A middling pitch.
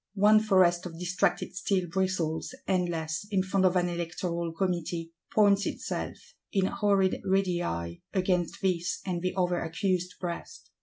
Yes: medium, 180 Hz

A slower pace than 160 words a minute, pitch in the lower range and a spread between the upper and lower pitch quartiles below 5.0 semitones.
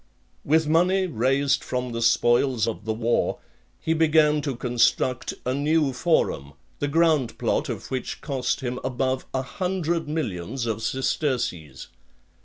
Yes: average, 140 wpm; low, 130 Hz; average, 4.6 semitones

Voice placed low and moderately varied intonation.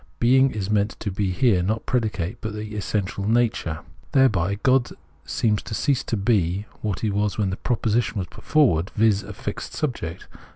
Yes: low, 105 Hz; average, 3.3 semitones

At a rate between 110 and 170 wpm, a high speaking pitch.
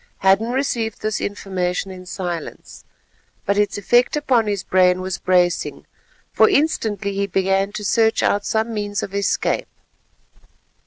Yes: average, 140 wpm; high, 200 Hz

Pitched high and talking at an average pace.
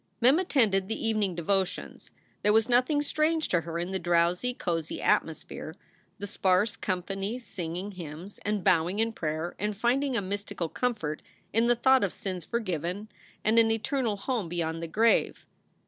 Yes: high, 200 Hz; average, 165 wpm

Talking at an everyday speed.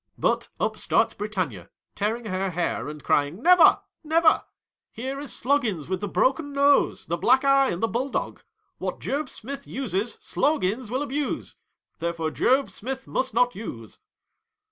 Yes: average, 160 wpm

